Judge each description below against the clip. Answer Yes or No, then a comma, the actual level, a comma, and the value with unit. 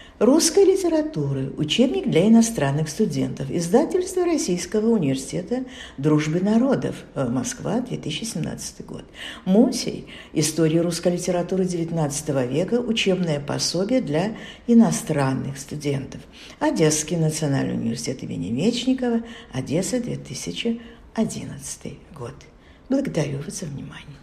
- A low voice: No, medium, 180 Hz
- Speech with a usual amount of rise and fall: No, wide, 7.6 semitones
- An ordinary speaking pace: No, slow, 90 wpm